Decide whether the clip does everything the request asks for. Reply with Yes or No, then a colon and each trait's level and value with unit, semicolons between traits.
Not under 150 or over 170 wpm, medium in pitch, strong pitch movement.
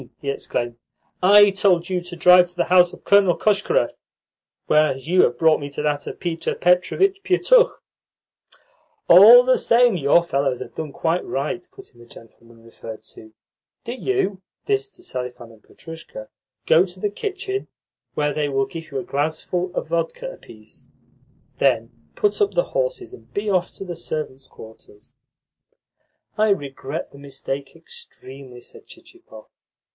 Yes: average, 160 wpm; medium, 175 Hz; wide, 7.1 semitones